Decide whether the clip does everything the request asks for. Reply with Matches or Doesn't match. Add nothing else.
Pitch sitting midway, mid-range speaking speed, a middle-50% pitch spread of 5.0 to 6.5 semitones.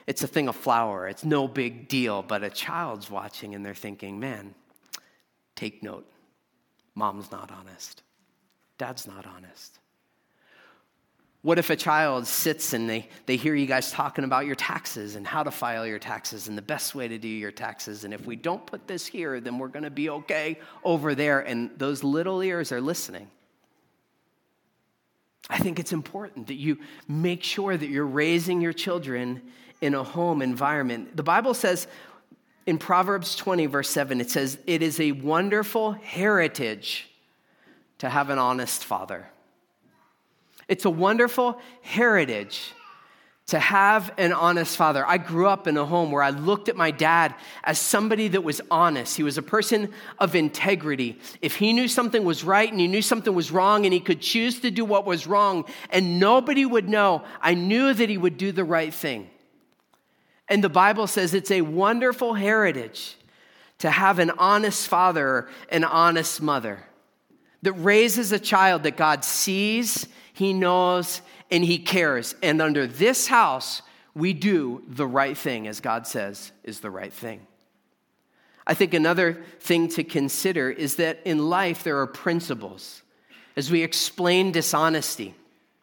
Matches